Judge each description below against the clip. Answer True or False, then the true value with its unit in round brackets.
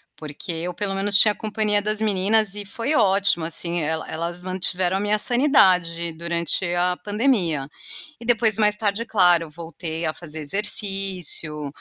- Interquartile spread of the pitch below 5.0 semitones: True (3.7 semitones)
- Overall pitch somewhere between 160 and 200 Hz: True (190 Hz)